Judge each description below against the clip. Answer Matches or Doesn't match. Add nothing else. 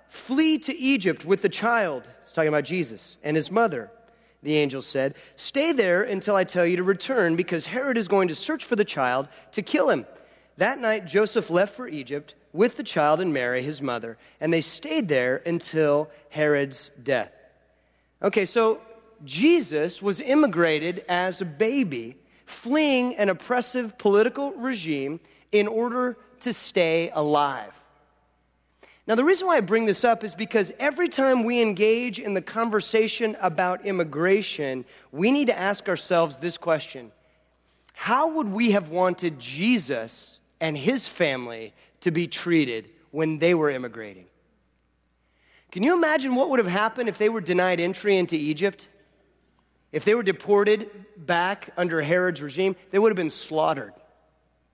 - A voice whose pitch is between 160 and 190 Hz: Matches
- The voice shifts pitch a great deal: Matches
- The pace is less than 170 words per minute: Matches